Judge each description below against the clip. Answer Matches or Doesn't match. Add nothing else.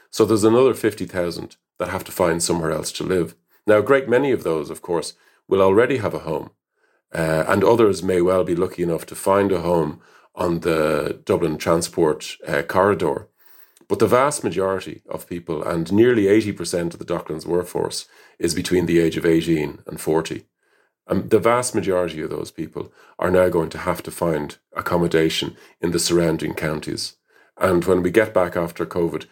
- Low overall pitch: Matches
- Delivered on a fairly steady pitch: Matches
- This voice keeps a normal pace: Matches